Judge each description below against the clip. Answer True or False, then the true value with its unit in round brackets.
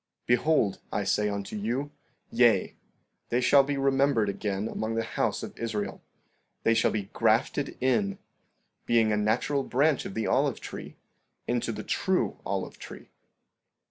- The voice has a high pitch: False (115 Hz)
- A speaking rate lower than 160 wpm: True (150 wpm)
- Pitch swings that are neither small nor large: True (4.4 semitones)